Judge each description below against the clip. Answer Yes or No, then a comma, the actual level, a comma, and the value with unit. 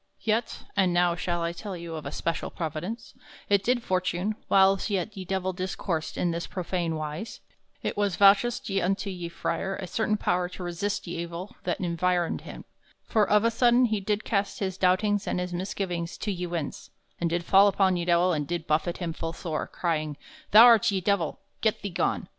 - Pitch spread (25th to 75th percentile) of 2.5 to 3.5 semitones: Yes, average, 2.9 semitones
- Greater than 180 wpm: Yes, average, 200 wpm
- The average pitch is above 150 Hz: Yes, medium, 185 Hz